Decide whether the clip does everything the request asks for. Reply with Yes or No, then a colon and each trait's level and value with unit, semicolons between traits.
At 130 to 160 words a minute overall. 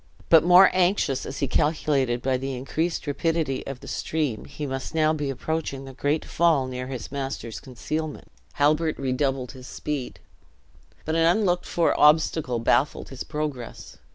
Yes: average, 155 wpm